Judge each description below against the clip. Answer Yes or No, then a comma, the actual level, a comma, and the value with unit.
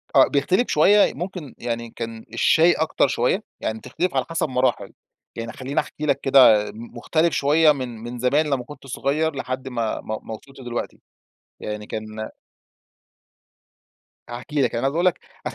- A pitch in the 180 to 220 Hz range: No, low, 130 Hz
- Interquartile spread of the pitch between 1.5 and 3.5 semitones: No, average, 4.5 semitones